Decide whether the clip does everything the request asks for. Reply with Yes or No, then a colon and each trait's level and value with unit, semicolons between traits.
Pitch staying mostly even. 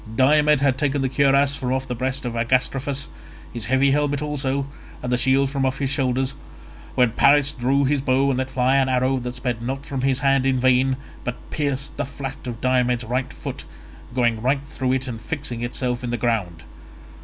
Yes: narrow, 1.8 semitones